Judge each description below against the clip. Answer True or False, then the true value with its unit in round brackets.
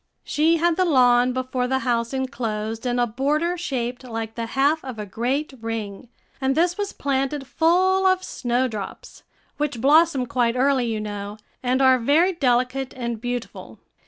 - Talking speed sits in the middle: True (160 wpm)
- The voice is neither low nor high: False (255 Hz)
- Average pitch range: True (3.8 semitones)